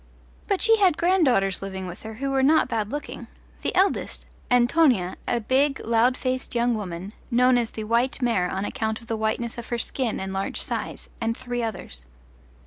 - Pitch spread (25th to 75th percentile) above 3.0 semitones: Yes, average, 3.5 semitones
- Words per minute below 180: No, average, 190 wpm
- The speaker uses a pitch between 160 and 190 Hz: No, high, 235 Hz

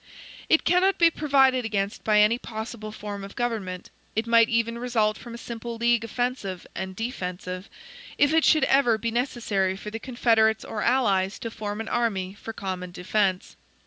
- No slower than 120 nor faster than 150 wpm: No, average, 175 wpm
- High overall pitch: Yes, high, 225 Hz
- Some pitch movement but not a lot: Yes, average, 3.2 semitones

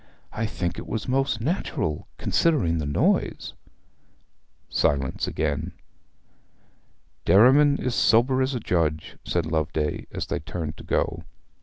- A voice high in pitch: No, very low, 95 Hz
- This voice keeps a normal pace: No, slow, 125 wpm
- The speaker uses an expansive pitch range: Yes, wide, 8.7 semitones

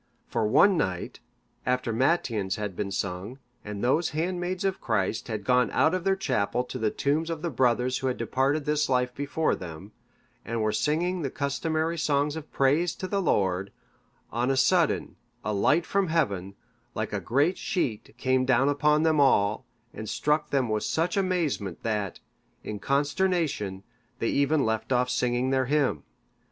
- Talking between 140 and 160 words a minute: No, average, 170 wpm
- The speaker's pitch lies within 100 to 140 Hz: Yes, low, 135 Hz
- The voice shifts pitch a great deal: Yes, wide, 6.4 semitones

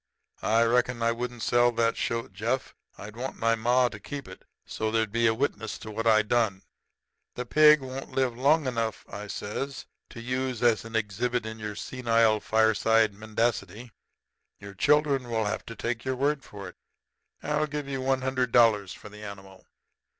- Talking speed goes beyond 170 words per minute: Yes, average, 180 wpm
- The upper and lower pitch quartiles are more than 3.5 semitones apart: No, average, 2.9 semitones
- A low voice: Yes, low, 115 Hz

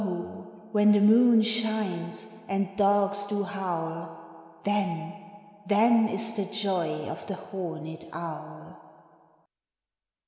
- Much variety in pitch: No, average, 3.7 semitones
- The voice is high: Yes, high, 200 Hz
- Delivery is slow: Yes, slow, 105 wpm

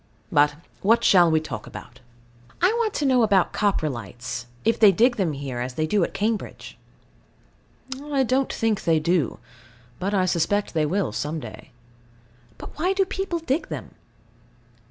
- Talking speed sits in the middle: Yes, average, 160 wpm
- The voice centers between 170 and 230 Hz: Yes, high, 190 Hz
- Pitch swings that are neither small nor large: No, wide, 7.8 semitones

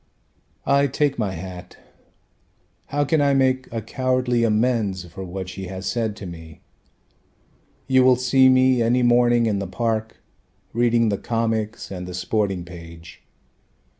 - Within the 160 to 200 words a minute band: No, average, 145 wpm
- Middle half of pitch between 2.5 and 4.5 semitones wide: No, average, 5.1 semitones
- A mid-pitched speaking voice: No, low, 115 Hz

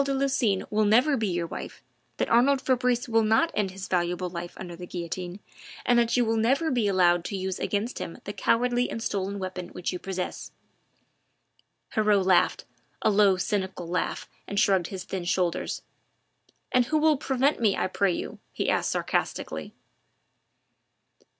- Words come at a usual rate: Yes, average, 170 wpm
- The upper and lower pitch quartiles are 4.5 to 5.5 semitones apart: Yes, average, 4.8 semitones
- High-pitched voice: Yes, high, 200 Hz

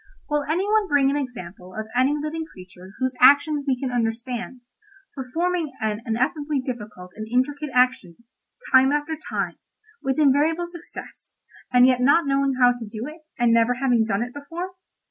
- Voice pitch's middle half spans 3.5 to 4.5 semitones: Yes, average, 3.9 semitones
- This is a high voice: Yes, very high, 260 Hz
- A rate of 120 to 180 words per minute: Yes, average, 165 wpm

